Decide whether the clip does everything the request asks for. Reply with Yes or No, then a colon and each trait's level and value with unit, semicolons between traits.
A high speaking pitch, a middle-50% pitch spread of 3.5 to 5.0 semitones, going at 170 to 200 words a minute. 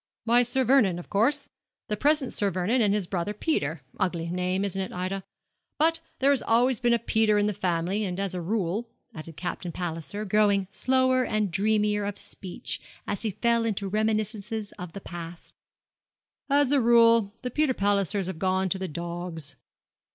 Yes: high, 205 Hz; average, 4.1 semitones; average, 180 wpm